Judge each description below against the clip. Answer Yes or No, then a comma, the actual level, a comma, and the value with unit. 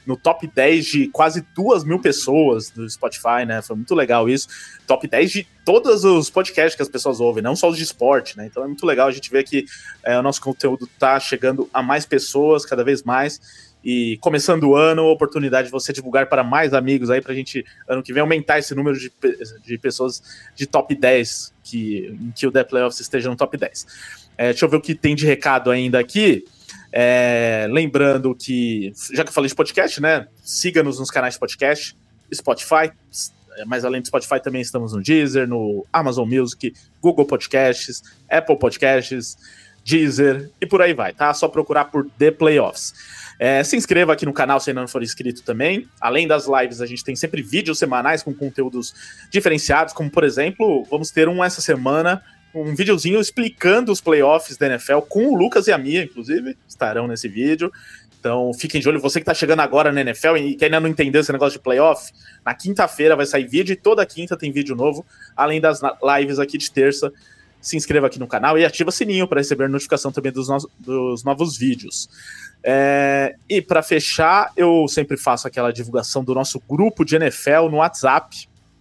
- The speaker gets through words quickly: Yes, fast, 200 wpm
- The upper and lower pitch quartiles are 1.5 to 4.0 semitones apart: Yes, average, 3.6 semitones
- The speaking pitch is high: No, medium, 140 Hz